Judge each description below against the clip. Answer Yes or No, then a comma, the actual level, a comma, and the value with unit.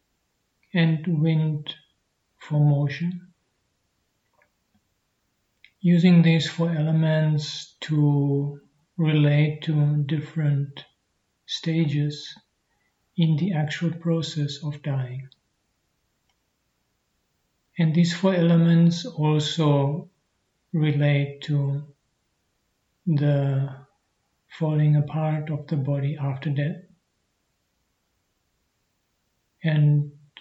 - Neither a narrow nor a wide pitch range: No, narrow, 2.1 semitones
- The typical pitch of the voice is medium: Yes, medium, 150 Hz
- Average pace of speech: No, slow, 70 wpm